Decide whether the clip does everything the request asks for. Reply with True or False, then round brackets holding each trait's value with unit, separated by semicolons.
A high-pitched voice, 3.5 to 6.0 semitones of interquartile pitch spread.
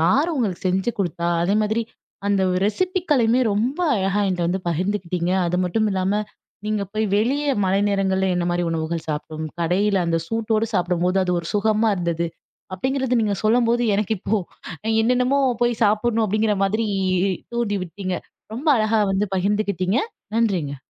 True (205 Hz; 3.8 semitones)